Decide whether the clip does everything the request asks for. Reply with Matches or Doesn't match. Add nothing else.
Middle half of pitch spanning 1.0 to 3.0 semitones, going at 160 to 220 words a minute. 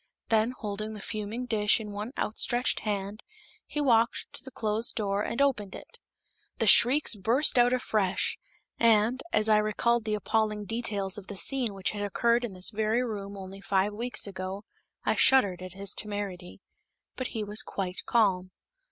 Matches